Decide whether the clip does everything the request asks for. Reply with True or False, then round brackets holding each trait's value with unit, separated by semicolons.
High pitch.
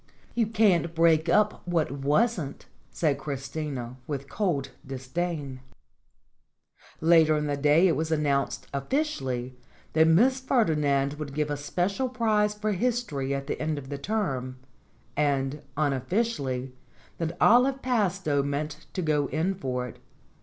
False (155 Hz)